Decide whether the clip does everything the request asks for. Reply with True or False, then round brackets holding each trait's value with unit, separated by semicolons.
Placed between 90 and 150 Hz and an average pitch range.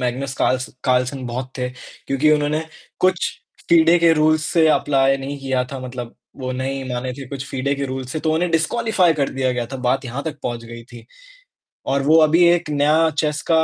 True (140 Hz; 3.5 semitones)